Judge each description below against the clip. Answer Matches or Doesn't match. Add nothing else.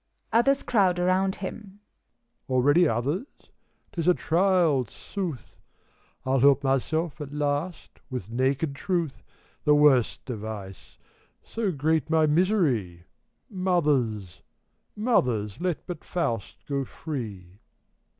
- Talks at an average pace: Doesn't match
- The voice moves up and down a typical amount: Doesn't match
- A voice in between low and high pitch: Matches